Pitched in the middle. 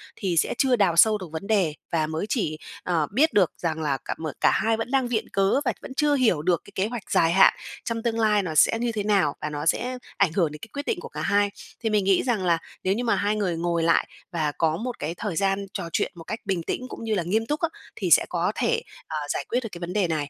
No: high, 195 Hz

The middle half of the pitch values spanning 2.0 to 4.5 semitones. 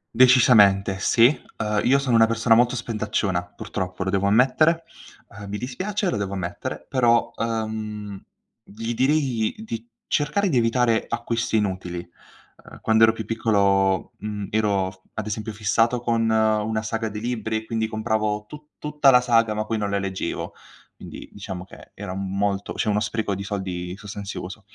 Yes: average, 2.7 semitones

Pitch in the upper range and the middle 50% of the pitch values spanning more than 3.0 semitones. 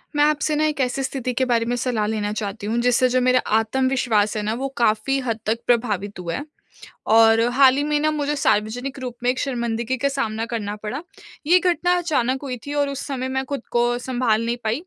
Yes: very high, 250 Hz; average, 3.6 semitones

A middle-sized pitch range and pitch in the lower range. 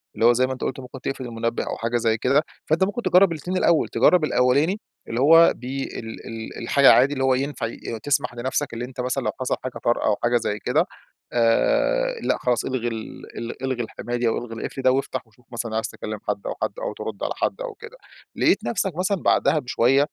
Yes: average, 3.8 semitones; low, 130 Hz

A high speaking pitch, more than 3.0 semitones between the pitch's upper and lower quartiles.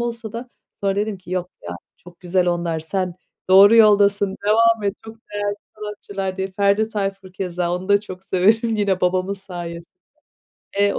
No: high, 195 Hz; narrow, 2.4 semitones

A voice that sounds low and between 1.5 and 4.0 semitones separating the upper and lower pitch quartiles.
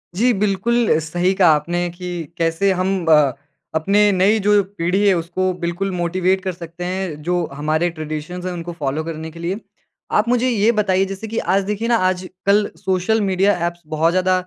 No: medium, 185 Hz; average, 2.8 semitones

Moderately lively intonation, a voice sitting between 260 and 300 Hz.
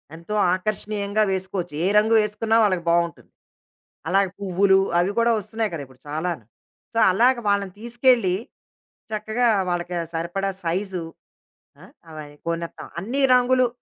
No: average, 3.9 semitones; high, 195 Hz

